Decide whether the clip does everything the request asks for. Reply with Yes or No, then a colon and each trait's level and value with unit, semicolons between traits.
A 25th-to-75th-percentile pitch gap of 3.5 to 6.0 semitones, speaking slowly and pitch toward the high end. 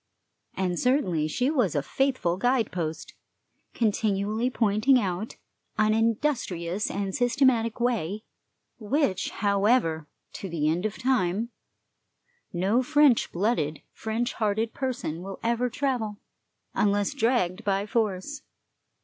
Yes: average, 4.7 semitones; slow, 115 wpm; high, 215 Hz